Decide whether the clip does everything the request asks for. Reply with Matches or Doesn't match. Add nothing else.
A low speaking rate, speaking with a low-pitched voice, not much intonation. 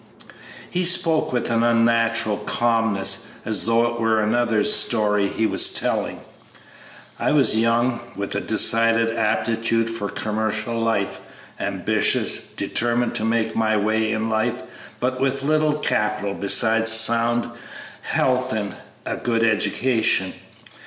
Matches